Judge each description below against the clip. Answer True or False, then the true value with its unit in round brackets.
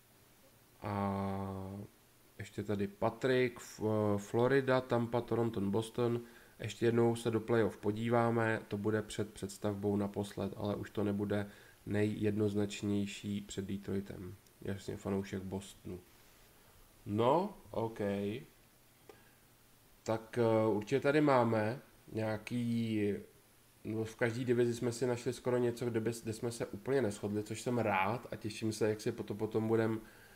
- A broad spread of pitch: False (2.5 semitones)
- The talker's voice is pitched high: False (110 Hz)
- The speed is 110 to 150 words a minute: True (120 wpm)